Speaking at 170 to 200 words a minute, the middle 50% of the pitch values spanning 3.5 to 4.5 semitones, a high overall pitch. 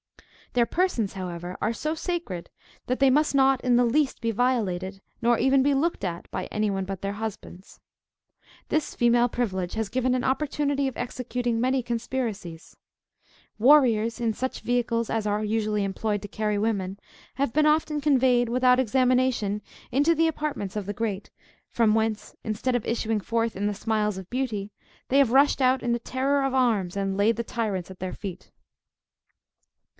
Yes: average, 175 wpm; average, 4.0 semitones; high, 235 Hz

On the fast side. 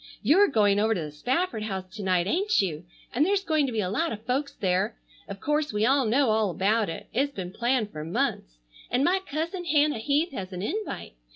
Yes: fast, 220 wpm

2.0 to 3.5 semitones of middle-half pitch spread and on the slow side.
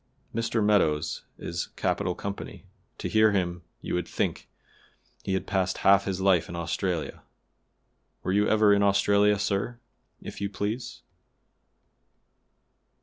Yes: narrow, 2.6 semitones; slow, 130 wpm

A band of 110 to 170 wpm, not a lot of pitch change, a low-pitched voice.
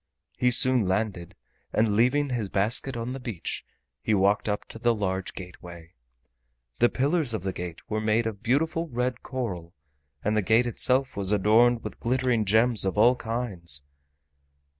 No: average, 160 wpm; average, 4.2 semitones; low, 110 Hz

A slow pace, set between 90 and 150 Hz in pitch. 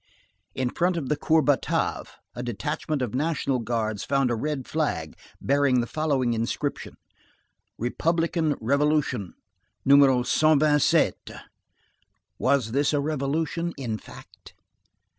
Yes: slow, 115 wpm; medium, 140 Hz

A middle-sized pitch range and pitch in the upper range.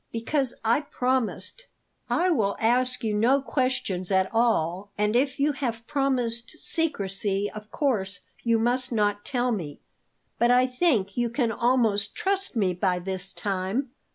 Yes: average, 4.3 semitones; high, 235 Hz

